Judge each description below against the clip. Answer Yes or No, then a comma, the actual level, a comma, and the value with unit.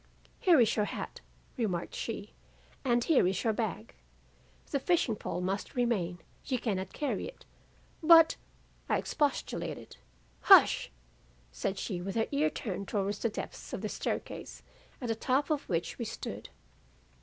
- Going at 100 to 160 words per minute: Yes, average, 155 wpm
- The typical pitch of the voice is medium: No, high, 225 Hz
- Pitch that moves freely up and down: Yes, wide, 6.0 semitones